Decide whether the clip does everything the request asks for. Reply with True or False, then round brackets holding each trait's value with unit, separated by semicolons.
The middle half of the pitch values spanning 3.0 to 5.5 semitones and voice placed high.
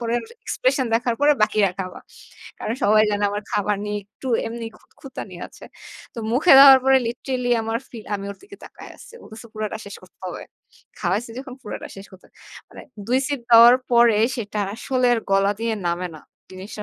True (3.6 semitones; 225 Hz)